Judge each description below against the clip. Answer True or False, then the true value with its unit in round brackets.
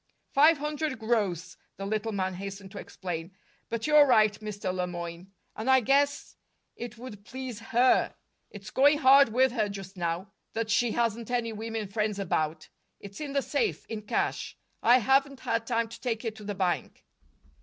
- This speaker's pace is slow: False (175 wpm)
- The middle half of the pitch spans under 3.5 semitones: False (4.5 semitones)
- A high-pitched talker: True (220 Hz)